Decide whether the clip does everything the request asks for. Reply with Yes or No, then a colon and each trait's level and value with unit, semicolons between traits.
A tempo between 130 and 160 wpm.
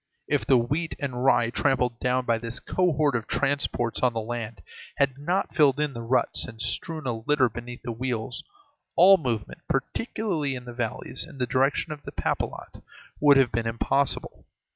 No: average, 175 wpm